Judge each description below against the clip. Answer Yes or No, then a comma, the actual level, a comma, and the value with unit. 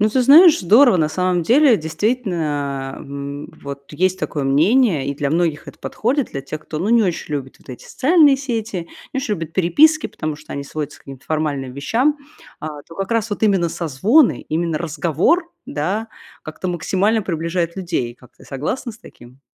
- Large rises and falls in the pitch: Yes, wide, 7.4 semitones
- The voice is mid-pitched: Yes, medium, 170 Hz